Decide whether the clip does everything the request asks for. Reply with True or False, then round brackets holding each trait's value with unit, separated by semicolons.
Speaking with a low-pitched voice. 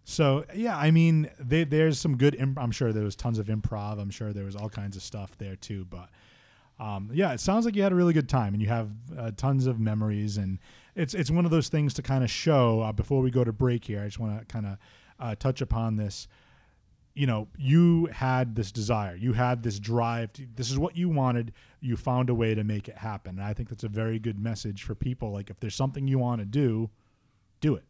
True (115 Hz)